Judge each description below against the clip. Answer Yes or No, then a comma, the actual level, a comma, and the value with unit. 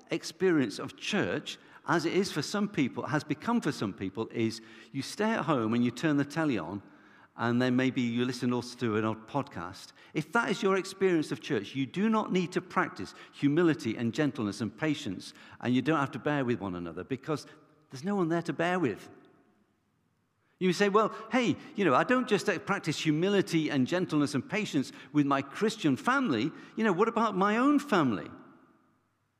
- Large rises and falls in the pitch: Yes, wide, 7.1 semitones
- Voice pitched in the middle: Yes, medium, 155 Hz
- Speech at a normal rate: Yes, average, 195 wpm